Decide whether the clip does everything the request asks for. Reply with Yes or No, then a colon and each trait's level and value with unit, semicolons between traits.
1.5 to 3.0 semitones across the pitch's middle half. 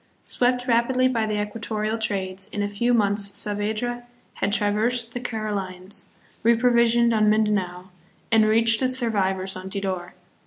Yes: average, 2.7 semitones